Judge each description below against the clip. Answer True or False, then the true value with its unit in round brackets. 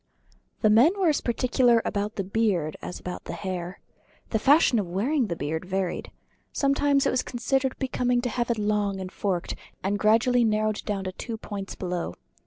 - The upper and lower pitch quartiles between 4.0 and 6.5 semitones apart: True (4.4 semitones)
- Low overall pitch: False (215 Hz)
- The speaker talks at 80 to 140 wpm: False (180 wpm)